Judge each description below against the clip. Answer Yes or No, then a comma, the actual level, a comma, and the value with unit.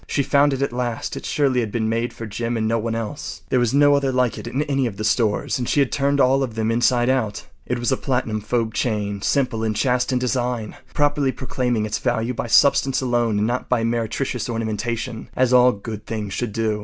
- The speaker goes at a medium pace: No, fast, 230 wpm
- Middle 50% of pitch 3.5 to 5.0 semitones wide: No, narrow, 2.6 semitones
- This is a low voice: Yes, low, 120 Hz